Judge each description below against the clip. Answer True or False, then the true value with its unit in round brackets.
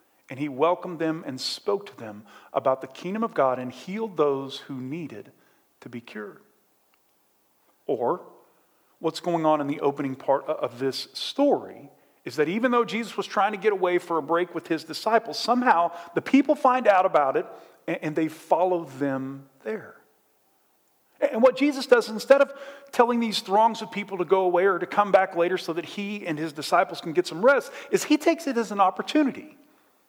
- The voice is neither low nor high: True (180 Hz)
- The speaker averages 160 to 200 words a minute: True (190 wpm)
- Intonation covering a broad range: True (6.8 semitones)